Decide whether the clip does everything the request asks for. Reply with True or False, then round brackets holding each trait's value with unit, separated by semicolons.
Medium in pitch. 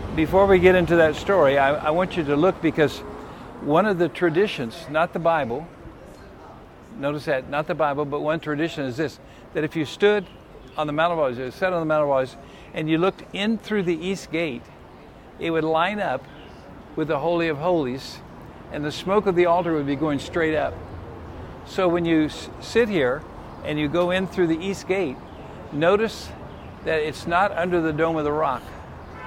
True (160 Hz)